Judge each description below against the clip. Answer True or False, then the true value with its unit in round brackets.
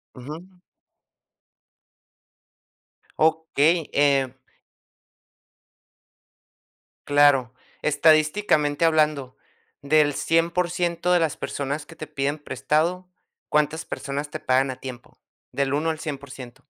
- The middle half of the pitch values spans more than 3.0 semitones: False (2.5 semitones)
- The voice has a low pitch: False (150 Hz)